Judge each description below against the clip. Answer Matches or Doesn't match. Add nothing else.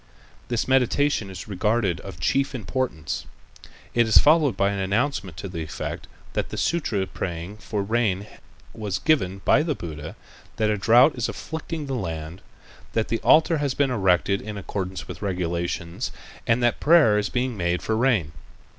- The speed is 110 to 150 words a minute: Doesn't match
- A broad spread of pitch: Matches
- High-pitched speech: Doesn't match